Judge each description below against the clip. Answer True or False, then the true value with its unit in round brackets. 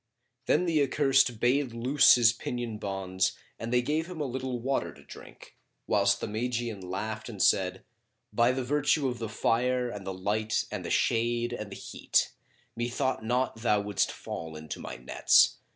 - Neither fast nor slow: True (175 wpm)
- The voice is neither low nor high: False (120 Hz)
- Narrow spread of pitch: False (3.5 semitones)